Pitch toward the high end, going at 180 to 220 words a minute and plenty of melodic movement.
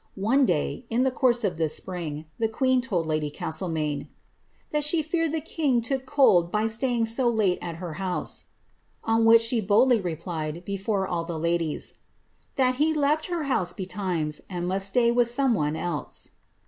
Yes: high, 210 Hz; average, 185 wpm; wide, 6.9 semitones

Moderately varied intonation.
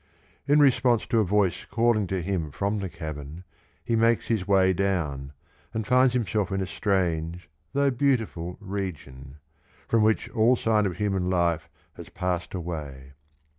Yes: average, 4.8 semitones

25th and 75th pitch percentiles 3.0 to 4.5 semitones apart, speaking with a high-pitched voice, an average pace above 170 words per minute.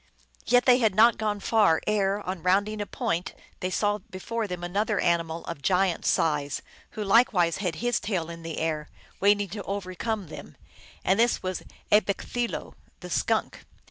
Yes: average, 3.6 semitones; high, 195 Hz; average, 180 wpm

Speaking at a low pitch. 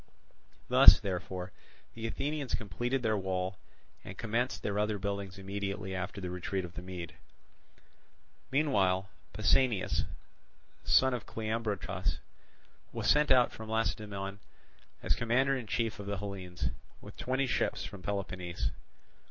Yes: low, 100 Hz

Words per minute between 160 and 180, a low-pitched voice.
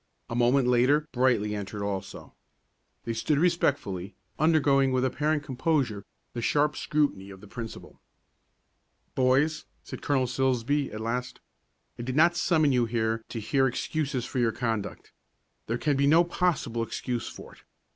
No: average, 150 wpm; low, 130 Hz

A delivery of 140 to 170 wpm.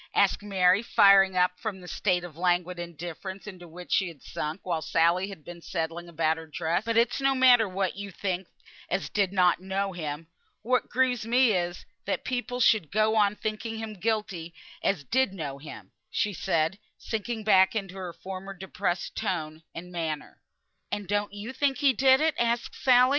No: average, 185 wpm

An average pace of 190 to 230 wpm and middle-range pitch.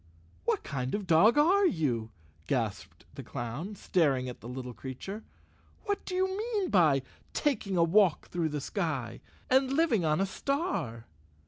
No: average, 165 wpm; medium, 175 Hz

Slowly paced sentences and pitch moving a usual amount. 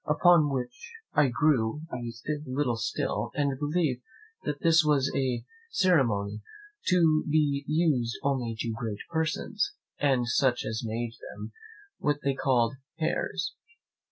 Yes: slow, 125 wpm; average, 4.4 semitones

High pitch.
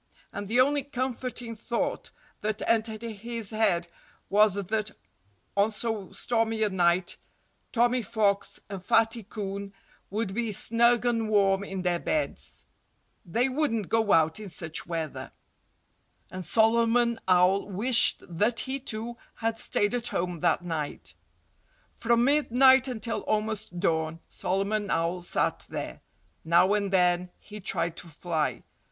Yes: high, 215 Hz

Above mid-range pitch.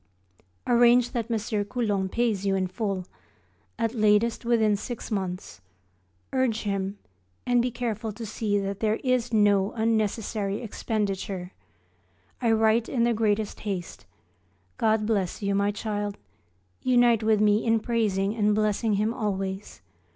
Yes: high, 215 Hz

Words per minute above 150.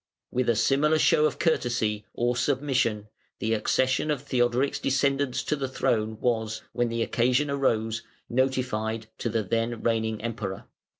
No: average, 145 wpm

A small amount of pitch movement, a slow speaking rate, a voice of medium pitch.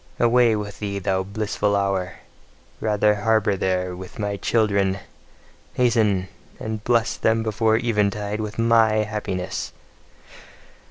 No: narrow, 2.0 semitones; slow, 115 wpm; low, 105 Hz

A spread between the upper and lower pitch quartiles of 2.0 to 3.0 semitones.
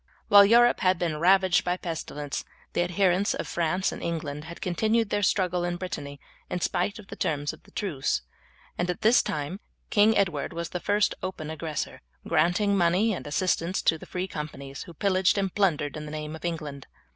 No: average, 3.8 semitones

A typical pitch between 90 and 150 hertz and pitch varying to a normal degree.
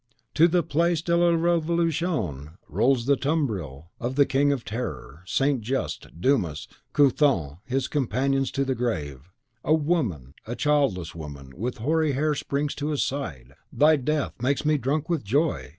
No: low, 135 Hz; wide, 8.8 semitones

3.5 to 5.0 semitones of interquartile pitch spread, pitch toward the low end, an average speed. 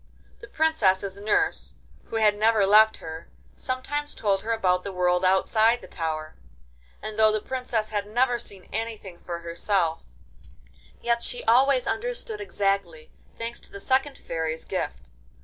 No: average, 4.7 semitones; high, 210 Hz; average, 150 wpm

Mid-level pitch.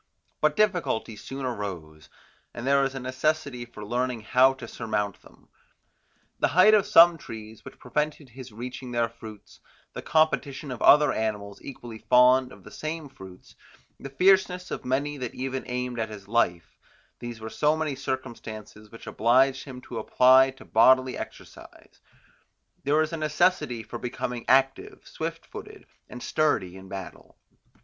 No: low, 125 Hz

